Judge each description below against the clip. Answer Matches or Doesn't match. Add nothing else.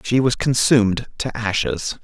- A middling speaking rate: Matches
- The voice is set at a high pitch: Doesn't match